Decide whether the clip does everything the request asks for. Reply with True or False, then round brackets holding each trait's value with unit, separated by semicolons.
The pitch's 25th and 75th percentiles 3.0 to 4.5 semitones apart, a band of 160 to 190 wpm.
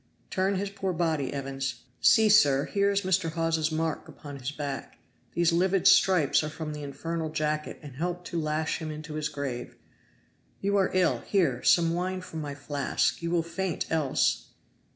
True (3.7 semitones; 175 wpm)